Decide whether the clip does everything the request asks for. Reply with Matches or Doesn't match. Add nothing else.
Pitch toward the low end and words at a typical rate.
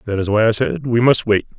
Doesn't match